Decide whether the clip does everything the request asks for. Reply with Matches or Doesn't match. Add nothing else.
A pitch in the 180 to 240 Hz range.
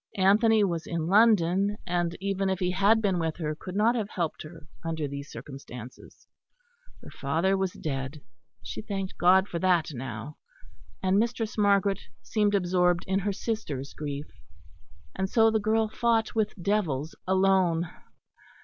Matches